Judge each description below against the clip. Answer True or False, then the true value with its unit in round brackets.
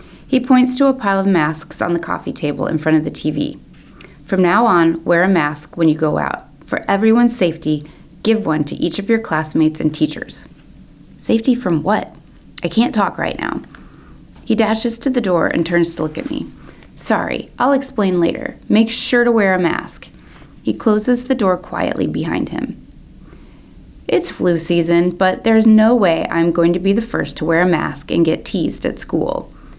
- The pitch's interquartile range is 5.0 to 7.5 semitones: True (5.3 semitones)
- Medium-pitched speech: True (180 Hz)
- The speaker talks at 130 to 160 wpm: False (195 wpm)